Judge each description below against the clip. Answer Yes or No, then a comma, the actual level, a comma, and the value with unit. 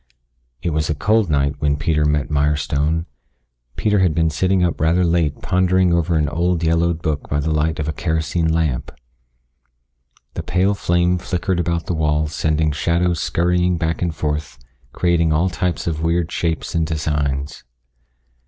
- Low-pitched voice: Yes, very low, 80 Hz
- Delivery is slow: No, average, 160 wpm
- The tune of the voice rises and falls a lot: No, narrow, 2.4 semitones